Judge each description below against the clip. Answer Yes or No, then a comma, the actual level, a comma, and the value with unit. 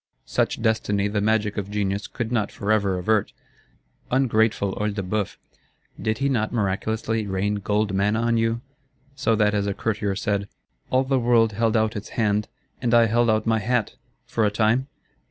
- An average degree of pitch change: No, narrow, 1.9 semitones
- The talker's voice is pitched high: No, low, 110 Hz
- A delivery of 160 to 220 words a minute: Yes, average, 170 wpm